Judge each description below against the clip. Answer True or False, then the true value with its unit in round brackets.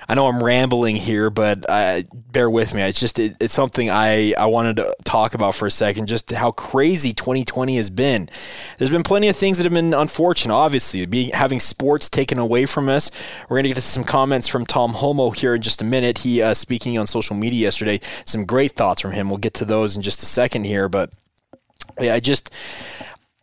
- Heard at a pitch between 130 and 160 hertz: False (120 Hz)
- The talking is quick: True (220 wpm)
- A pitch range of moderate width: True (3.6 semitones)